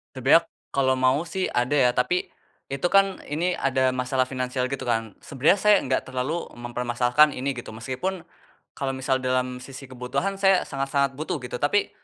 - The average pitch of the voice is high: No, low, 130 Hz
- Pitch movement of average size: Yes, average, 3.1 semitones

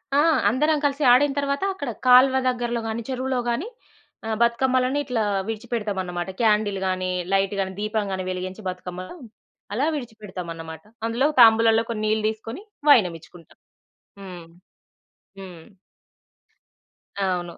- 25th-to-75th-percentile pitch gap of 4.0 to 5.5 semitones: Yes, average, 5.2 semitones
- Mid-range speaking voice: No, high, 220 Hz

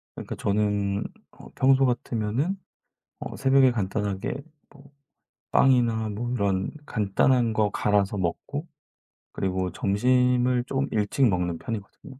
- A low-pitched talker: Yes, low, 110 Hz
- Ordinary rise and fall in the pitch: Yes, average, 4.2 semitones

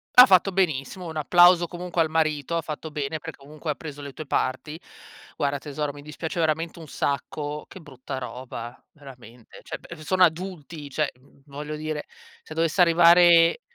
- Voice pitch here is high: No, medium, 155 Hz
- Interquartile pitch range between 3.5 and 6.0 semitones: No, average, 2.8 semitones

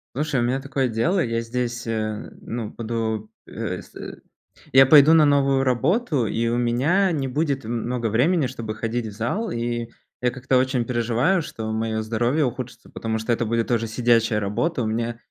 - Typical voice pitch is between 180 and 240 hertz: No, low, 120 Hz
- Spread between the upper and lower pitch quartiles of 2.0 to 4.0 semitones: Yes, average, 2.9 semitones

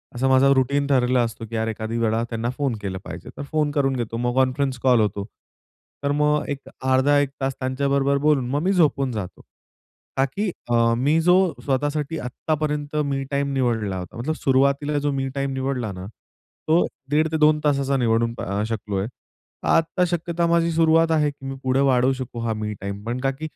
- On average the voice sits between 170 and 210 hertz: No, low, 135 Hz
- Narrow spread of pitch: No, average, 3.7 semitones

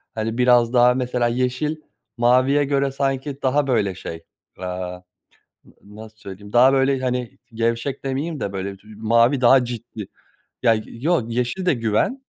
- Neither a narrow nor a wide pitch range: Yes, average, 3.4 semitones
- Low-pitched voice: Yes, low, 125 Hz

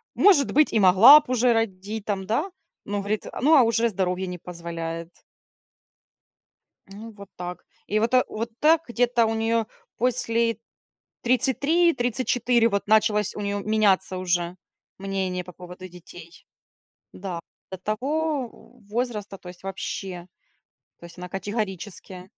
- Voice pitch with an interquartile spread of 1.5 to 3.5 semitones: No, average, 4.2 semitones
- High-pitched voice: Yes, high, 210 Hz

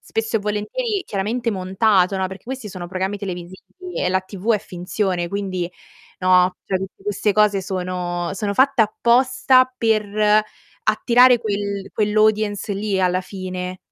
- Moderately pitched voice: No, high, 200 Hz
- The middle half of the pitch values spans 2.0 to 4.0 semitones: Yes, average, 2.7 semitones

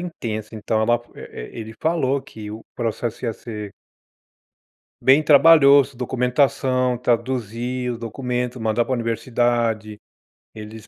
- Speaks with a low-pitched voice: Yes, low, 120 Hz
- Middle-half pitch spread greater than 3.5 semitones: No, narrow, 2.6 semitones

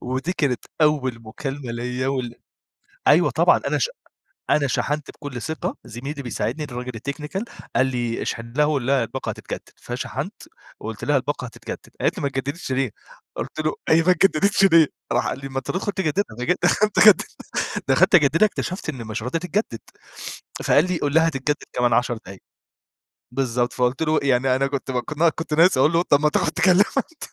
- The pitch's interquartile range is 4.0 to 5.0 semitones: Yes, average, 4.3 semitones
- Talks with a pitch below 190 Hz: Yes, medium, 140 Hz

